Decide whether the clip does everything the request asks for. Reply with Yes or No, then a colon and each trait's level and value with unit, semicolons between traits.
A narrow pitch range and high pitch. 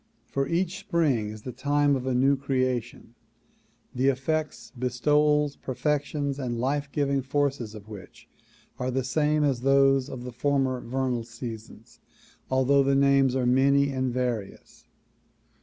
No: narrow, 2.3 semitones; low, 135 Hz